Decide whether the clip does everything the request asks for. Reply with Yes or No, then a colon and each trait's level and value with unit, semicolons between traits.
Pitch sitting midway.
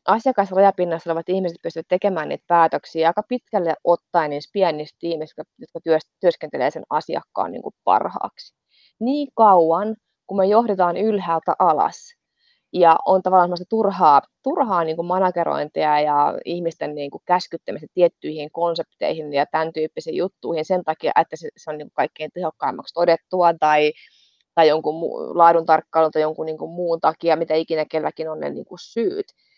Yes: medium, 170 Hz